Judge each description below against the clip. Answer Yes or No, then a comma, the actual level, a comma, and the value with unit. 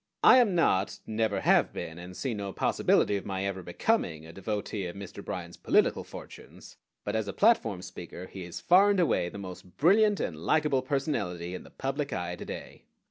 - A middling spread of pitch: No, wide, 8.2 semitones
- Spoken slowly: No, average, 195 wpm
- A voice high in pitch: No, low, 100 Hz